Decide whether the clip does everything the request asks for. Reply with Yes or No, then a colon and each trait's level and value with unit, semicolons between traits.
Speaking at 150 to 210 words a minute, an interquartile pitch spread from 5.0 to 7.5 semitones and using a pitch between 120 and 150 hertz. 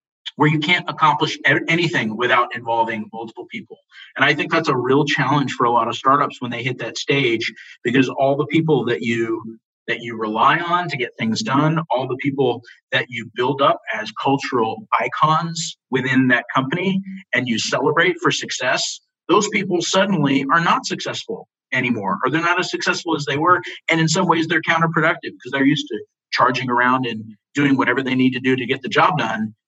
Yes: average, 195 wpm; wide, 5.6 semitones; medium, 140 Hz